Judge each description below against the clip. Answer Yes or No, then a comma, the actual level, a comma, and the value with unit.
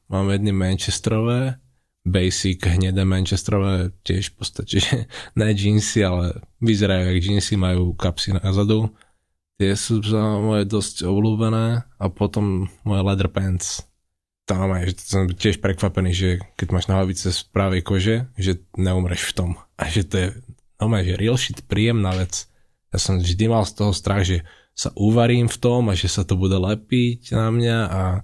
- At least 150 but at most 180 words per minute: Yes, fast, 165 wpm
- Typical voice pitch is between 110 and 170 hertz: No, very low, 95 Hz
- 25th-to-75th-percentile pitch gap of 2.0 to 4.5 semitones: Yes, average, 2.7 semitones